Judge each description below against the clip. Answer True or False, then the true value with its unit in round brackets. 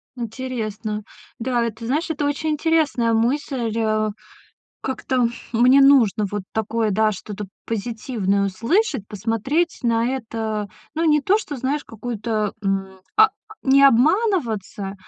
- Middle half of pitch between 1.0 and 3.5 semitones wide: False (4.5 semitones)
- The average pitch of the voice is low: False (235 Hz)